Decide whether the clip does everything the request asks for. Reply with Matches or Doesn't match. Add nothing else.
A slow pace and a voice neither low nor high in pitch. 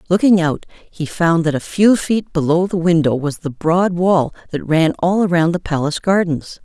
Doesn't match